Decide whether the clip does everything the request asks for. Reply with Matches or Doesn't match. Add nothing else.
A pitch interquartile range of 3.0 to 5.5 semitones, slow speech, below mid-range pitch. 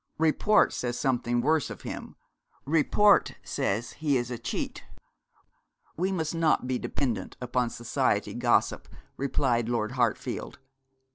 Matches